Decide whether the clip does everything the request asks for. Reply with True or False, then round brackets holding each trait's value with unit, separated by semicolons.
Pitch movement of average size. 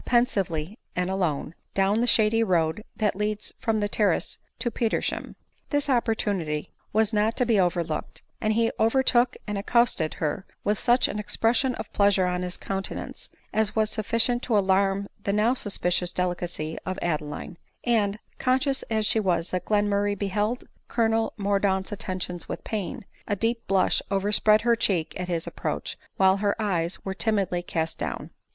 True (3.4 semitones)